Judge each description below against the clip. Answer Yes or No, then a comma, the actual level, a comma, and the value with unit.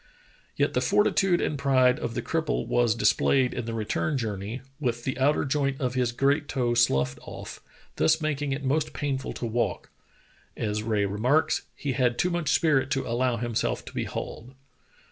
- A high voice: No, low, 130 Hz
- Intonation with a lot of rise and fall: No, average, 3.3 semitones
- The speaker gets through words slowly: No, average, 185 wpm